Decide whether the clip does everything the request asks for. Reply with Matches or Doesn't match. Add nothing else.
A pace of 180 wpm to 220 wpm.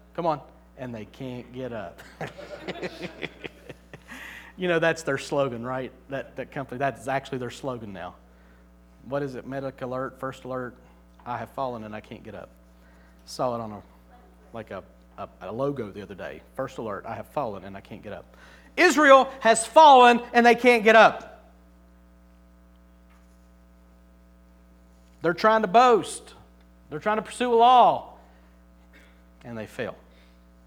Doesn't match